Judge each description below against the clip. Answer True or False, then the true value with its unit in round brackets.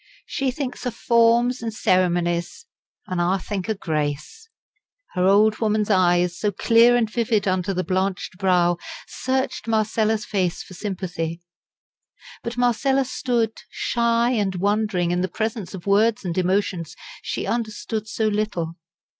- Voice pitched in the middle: False (205 Hz)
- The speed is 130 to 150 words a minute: True (140 wpm)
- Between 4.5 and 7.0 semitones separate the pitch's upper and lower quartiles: False (4.1 semitones)